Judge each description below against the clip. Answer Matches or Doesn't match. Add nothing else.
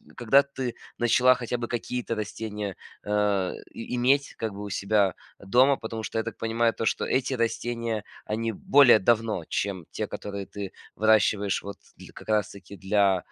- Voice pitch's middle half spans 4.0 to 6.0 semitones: Doesn't match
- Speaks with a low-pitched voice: Matches